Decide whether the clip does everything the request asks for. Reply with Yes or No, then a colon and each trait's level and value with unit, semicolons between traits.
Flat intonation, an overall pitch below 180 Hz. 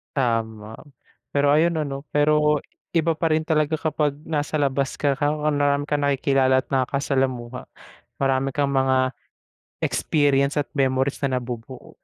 Yes: narrow, 2.1 semitones; medium, 140 Hz